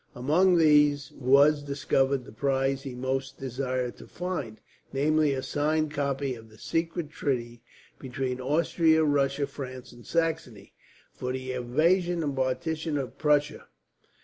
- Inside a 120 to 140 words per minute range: Yes, slow, 135 wpm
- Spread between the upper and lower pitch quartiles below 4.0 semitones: Yes, average, 3.1 semitones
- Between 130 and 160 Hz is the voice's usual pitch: Yes, medium, 140 Hz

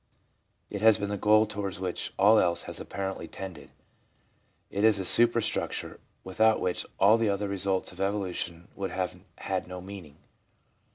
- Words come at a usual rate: Yes, average, 160 wpm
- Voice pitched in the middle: No, low, 100 Hz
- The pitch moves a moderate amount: No, narrow, 2.1 semitones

